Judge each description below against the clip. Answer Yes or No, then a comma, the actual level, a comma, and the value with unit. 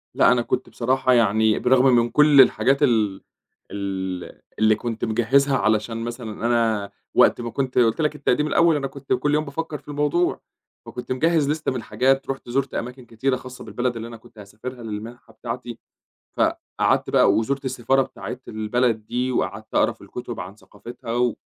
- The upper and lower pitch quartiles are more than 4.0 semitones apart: No, average, 3.3 semitones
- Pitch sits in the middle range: No, low, 125 Hz